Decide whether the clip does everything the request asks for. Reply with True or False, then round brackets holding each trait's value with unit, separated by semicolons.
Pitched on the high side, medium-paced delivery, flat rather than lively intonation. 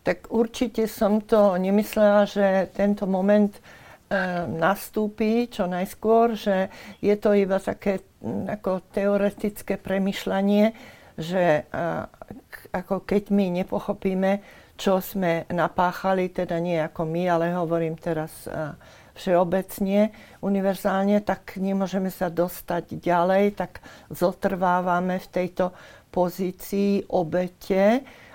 False (195 Hz; 100 wpm; 2.2 semitones)